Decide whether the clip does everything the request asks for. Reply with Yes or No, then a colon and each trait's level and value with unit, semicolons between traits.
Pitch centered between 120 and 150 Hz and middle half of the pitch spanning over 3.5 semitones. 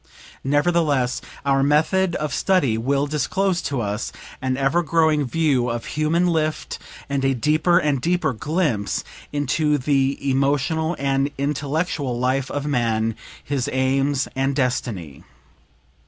No: medium, 140 Hz; average, 3.0 semitones